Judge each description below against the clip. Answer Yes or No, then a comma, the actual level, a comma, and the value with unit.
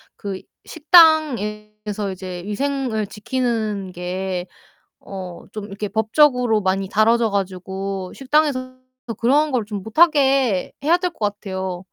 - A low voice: No, high, 210 Hz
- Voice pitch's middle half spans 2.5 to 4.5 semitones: No, average, 5.3 semitones